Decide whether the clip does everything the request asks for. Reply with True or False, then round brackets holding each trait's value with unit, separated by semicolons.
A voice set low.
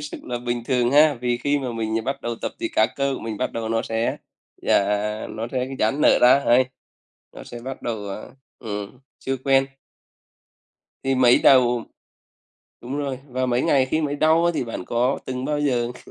True (125 Hz)